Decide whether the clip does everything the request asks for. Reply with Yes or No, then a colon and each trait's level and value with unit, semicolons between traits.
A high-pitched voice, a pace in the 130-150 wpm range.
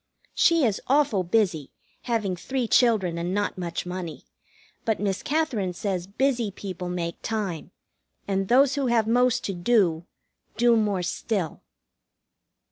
Yes: high, 205 Hz; slow, 135 wpm